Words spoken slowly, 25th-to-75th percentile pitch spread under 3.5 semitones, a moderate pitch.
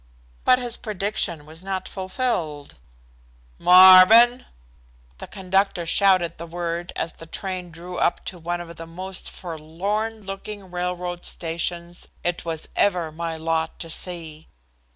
Yes: slow, 130 wpm; narrow, 2.5 semitones; medium, 175 Hz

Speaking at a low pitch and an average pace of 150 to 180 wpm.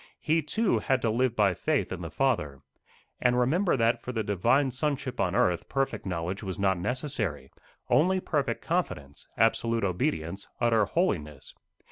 Yes: low, 115 Hz; average, 155 wpm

